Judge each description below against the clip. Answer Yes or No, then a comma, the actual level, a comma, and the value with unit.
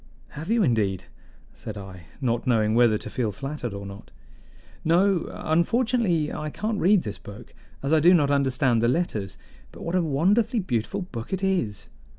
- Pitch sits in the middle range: Yes, medium, 145 Hz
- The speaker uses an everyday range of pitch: No, wide, 8.2 semitones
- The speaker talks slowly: No, average, 170 wpm